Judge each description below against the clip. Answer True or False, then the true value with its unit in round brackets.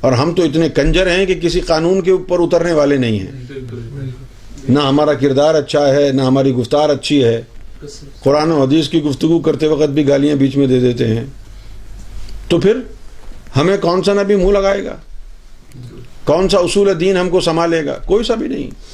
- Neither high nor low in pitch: True (145 Hz)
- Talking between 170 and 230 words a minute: True (190 wpm)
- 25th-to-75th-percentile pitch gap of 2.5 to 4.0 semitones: False (4.9 semitones)